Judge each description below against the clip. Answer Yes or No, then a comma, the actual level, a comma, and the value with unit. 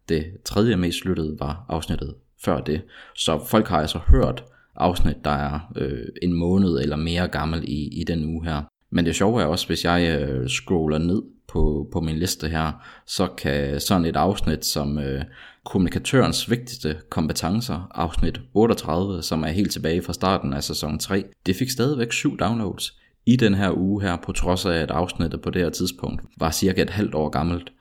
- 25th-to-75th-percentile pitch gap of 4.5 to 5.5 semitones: No, average, 3.6 semitones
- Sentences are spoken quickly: No, average, 190 wpm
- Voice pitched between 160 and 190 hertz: No, very low, 85 Hz